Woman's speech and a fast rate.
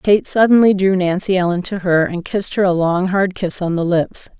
Yes: female; fast, 230 wpm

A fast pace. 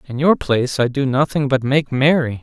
Yes: fast, 225 wpm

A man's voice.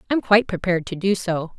No: female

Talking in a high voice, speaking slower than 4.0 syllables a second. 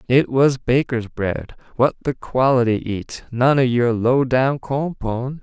No: low, 125 Hz; 3.7 syllables/s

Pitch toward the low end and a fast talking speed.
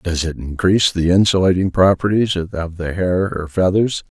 No: very low, 90 Hz; average, 155 wpm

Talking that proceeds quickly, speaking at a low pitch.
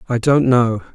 No: average, 190 wpm; low, 120 Hz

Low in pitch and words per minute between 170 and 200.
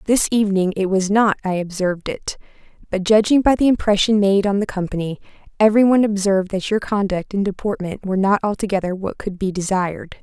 No: high, 200 Hz; average, 180 wpm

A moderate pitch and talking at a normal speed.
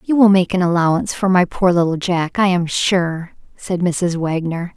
Yes: medium, 180 Hz; average, 190 wpm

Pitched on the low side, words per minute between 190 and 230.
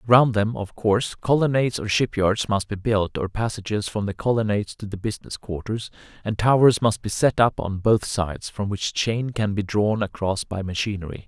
Yes: low, 105 Hz; average, 195 wpm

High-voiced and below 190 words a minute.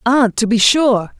No: high, 235 Hz; average, 200 wpm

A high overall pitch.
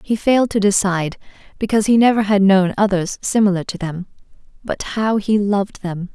Yes: high, 200 Hz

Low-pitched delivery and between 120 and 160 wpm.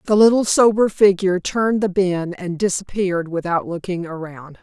No: medium, 185 Hz; average, 155 wpm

